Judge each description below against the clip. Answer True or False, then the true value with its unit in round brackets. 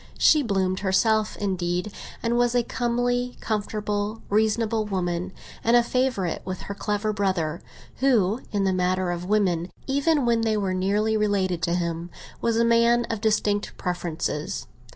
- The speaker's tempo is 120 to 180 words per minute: True (150 wpm)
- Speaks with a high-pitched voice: True (210 Hz)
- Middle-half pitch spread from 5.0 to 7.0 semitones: False (3.9 semitones)